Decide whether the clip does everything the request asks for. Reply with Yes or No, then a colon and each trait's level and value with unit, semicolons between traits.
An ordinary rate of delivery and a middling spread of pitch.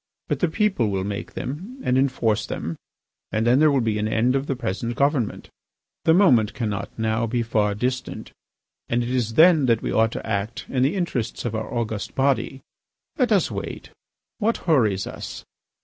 Yes: average, 185 wpm; average, 4.2 semitones